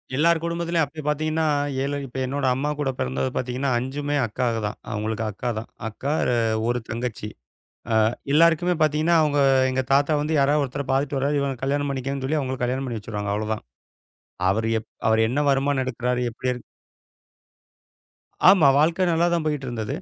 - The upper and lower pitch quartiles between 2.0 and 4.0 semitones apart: Yes, average, 3.6 semitones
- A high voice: No, low, 135 Hz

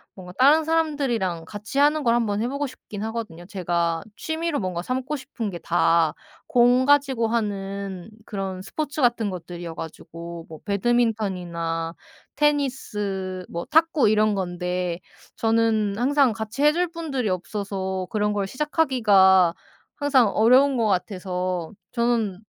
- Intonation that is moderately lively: No, wide, 5.9 semitones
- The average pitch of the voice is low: No, high, 210 Hz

